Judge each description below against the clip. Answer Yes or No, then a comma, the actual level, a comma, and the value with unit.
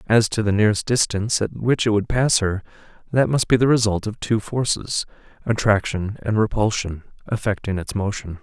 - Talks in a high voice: No, low, 105 Hz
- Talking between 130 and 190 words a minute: Yes, average, 180 wpm